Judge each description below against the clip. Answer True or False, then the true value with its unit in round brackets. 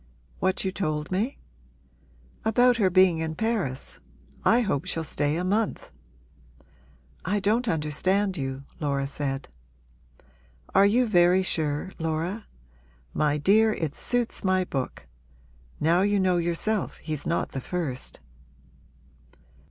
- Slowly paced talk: True (120 wpm)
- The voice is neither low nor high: True (180 Hz)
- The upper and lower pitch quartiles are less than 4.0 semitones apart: False (5.2 semitones)